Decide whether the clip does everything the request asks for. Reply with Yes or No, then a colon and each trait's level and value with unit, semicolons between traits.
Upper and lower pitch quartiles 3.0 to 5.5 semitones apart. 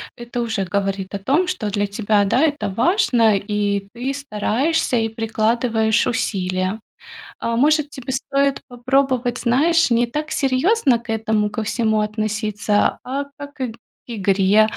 Yes: average, 4.2 semitones